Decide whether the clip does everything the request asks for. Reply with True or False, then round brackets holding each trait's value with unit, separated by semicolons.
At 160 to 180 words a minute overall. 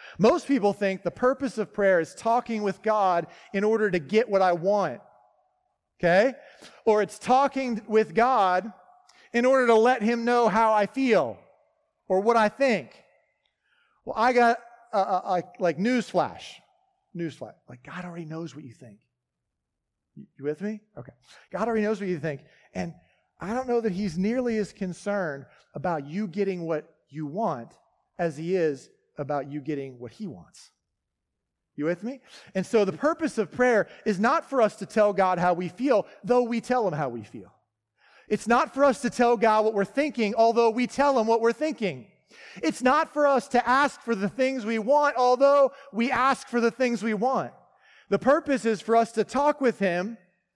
False (190 wpm)